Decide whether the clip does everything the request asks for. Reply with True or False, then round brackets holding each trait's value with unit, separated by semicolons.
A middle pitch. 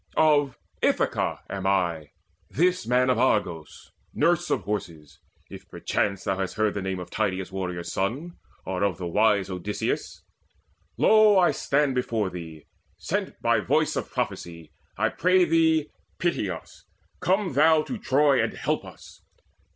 False (105 Hz)